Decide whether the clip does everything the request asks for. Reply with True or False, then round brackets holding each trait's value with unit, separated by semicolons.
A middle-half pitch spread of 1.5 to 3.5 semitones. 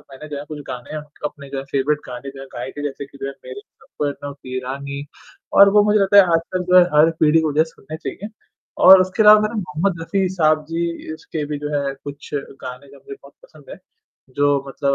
False (4.0 semitones)